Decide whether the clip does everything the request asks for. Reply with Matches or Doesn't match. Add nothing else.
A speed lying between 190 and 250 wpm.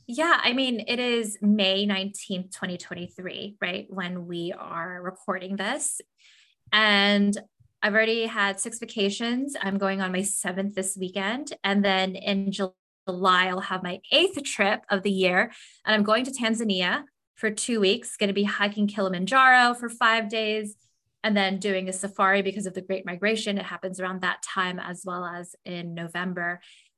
Doesn't match